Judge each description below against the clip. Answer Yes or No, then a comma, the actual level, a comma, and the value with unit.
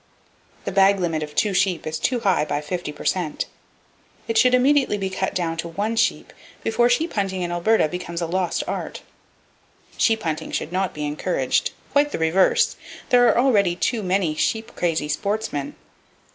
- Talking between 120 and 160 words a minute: No, average, 170 wpm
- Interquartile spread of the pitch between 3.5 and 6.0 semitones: Yes, average, 5.2 semitones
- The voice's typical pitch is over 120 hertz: Yes, high, 190 Hz